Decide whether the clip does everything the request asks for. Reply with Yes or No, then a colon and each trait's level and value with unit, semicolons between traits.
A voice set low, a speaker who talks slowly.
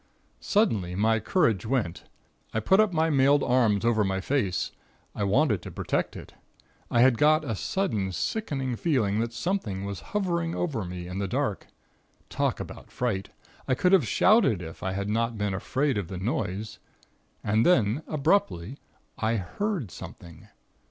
No: low, 115 Hz; average, 160 wpm